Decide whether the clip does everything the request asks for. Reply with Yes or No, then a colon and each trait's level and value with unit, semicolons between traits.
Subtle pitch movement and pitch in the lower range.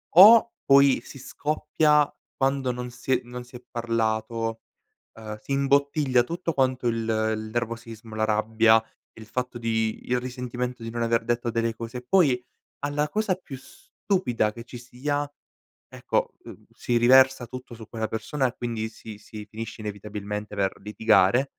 No: average, 3.1 semitones; low, 120 Hz